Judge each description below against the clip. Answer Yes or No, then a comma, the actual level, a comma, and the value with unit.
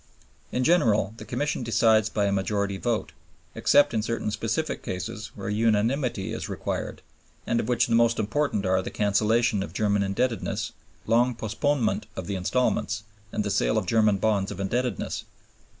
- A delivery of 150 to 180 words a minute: Yes, average, 160 wpm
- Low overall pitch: Yes, low, 110 Hz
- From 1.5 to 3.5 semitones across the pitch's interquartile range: Yes, average, 2.7 semitones